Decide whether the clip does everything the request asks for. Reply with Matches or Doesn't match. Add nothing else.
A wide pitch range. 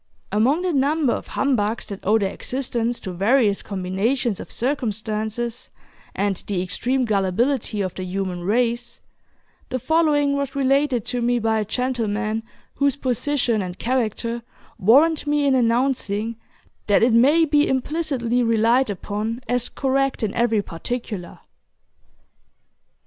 Doesn't match